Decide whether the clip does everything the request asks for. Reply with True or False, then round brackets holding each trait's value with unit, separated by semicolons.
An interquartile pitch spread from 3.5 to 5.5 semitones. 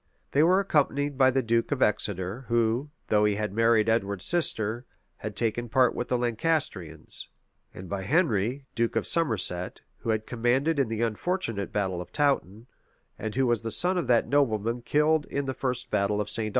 True (4.5 semitones)